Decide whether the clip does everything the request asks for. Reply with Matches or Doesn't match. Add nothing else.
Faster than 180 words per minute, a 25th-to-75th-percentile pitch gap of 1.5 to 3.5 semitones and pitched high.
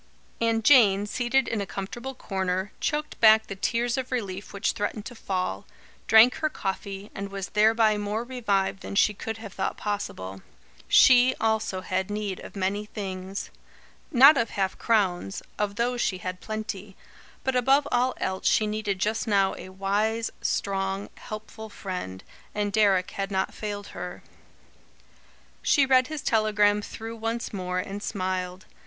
Doesn't match